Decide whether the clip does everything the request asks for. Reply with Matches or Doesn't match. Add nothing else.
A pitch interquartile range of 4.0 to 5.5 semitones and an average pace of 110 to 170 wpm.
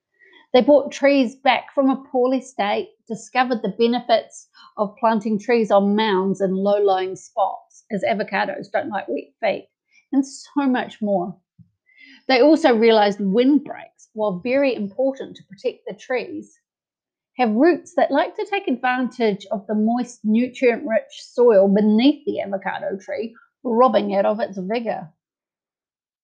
Matches